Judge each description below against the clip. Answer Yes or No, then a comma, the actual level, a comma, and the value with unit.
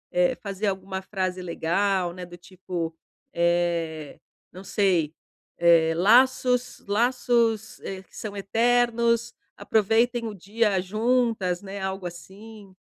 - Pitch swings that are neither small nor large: Yes, average, 4.1 semitones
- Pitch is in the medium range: No, high, 195 Hz